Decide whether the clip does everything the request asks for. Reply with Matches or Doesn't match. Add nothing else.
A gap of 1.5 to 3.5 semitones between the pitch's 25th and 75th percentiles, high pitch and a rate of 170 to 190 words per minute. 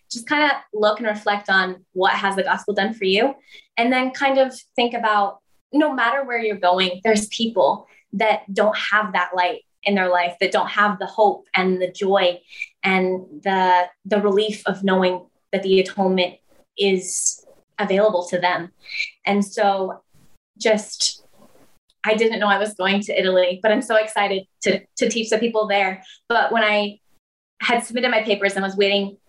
Matches